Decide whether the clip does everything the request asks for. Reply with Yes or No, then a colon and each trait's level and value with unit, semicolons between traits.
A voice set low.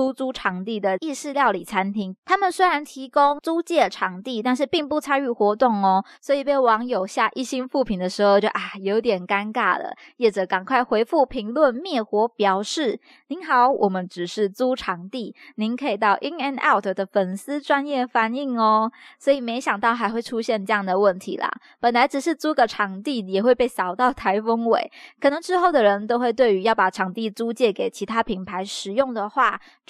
No: high, 235 Hz